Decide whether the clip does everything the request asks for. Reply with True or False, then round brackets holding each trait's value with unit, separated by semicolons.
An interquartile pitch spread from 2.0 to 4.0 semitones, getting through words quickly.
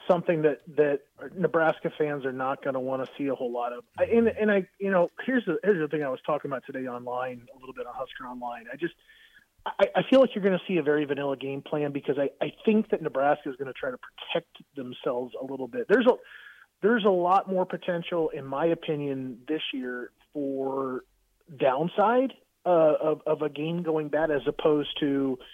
False (5.4 semitones; 220 wpm)